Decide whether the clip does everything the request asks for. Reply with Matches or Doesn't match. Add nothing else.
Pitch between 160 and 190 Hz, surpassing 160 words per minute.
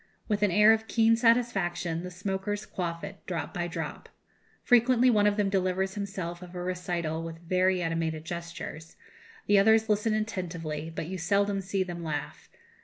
Matches